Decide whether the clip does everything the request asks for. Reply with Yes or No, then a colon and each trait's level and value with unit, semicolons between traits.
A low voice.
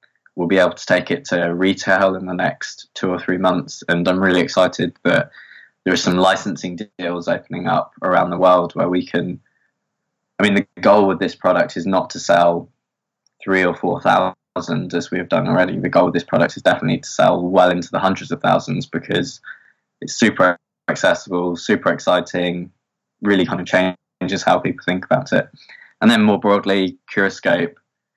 Yes: very low, 90 Hz